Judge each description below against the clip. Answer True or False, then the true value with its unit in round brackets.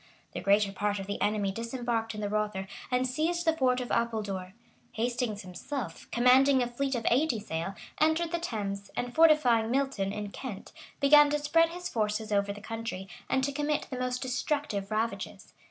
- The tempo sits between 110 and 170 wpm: False (180 wpm)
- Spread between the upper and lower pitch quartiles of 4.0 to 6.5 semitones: True (5.0 semitones)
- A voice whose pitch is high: True (235 Hz)